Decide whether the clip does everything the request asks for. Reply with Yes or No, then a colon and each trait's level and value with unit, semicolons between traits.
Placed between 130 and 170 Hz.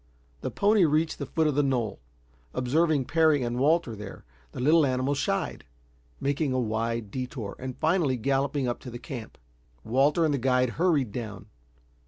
Yes: low, 135 Hz